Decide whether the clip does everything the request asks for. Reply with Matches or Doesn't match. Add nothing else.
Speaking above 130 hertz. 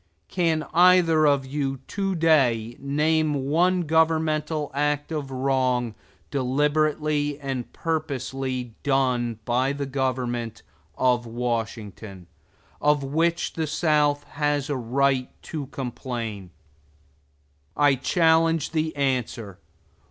Matches